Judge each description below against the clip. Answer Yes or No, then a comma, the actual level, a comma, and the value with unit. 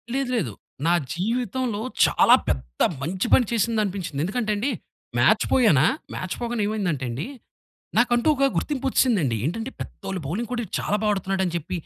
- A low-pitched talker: No, high, 205 Hz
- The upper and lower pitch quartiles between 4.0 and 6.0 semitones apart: Yes, wide, 5.6 semitones